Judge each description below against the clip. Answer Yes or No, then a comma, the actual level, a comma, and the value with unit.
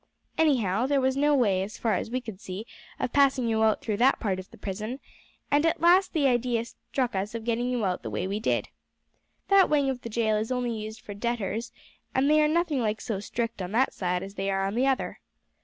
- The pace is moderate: No, fast, 240 wpm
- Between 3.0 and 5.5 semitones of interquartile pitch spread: Yes, average, 4.3 semitones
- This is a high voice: Yes, high, 230 Hz